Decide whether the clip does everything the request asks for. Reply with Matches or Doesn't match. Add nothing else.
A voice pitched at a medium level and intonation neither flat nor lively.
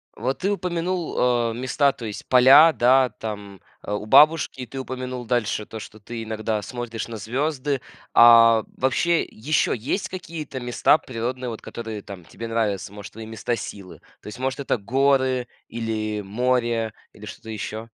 Doesn't match